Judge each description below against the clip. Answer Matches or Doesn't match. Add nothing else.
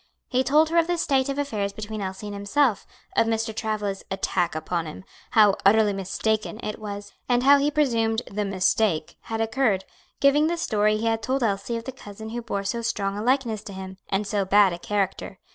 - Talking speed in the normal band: Doesn't match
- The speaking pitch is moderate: Doesn't match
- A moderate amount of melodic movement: Matches